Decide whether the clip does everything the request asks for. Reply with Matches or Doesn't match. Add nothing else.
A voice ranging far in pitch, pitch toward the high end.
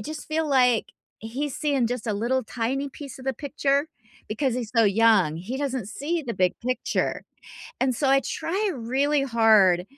Doesn't match